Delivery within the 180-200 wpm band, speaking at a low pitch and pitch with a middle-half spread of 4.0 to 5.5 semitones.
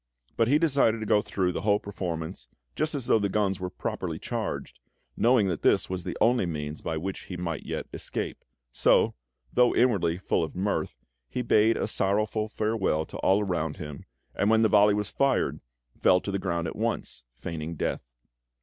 Yes: average, 190 wpm; low, 100 Hz; average, 4.4 semitones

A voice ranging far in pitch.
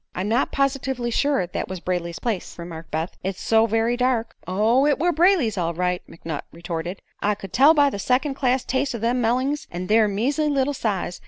Yes: wide, 6.7 semitones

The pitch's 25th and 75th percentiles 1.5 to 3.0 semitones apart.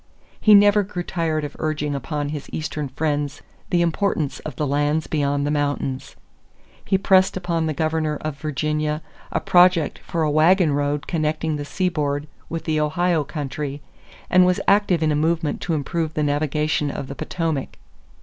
Yes: narrow, 2.4 semitones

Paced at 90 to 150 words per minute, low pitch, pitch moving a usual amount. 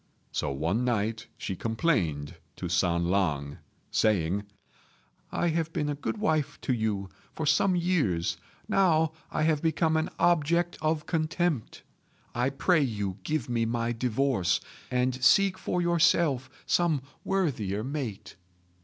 No: slow, 135 wpm; low, 130 Hz; wide, 7.9 semitones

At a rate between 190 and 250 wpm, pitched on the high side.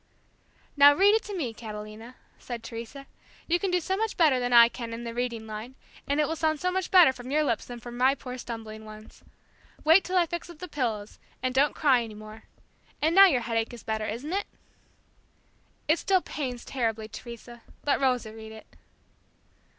Yes: average, 200 wpm; very high, 250 Hz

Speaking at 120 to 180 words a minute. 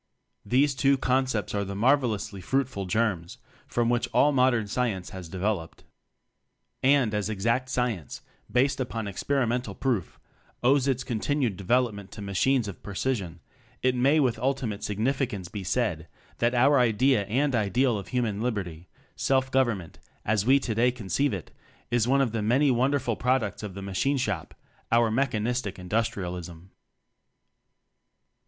Yes: average, 150 wpm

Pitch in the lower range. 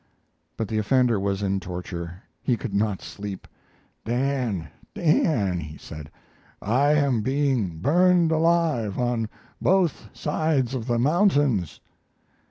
Yes: low, 120 Hz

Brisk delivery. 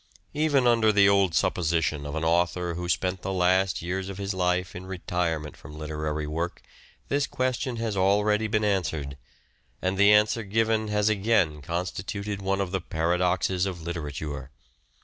No: average, 160 wpm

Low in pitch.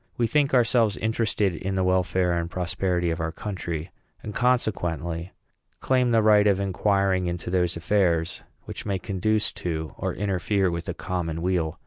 Yes: very low, 95 Hz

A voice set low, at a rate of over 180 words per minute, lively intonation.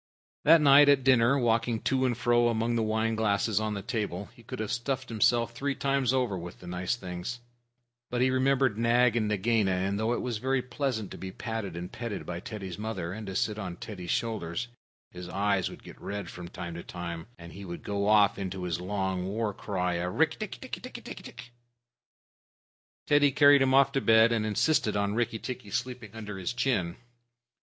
No: low, 110 Hz; average, 200 wpm; average, 4.2 semitones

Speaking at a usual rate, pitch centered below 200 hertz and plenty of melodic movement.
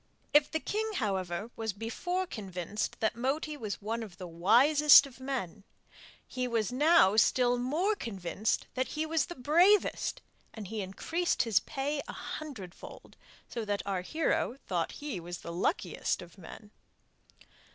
No: average, 155 wpm; high, 235 Hz; wide, 7.1 semitones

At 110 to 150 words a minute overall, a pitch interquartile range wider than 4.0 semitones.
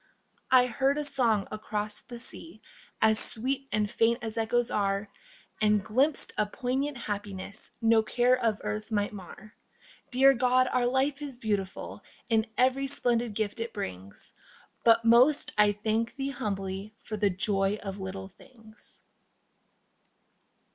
No: average, 140 wpm; average, 3.4 semitones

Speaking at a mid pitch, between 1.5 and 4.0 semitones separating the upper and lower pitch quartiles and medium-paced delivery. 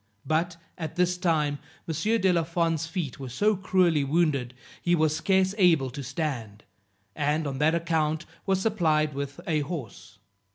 Yes: medium, 160 Hz; average, 3.4 semitones; average, 160 wpm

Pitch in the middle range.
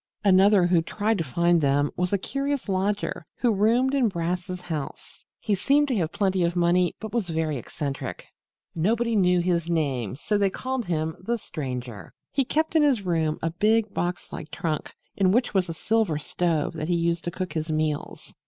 Yes: medium, 180 Hz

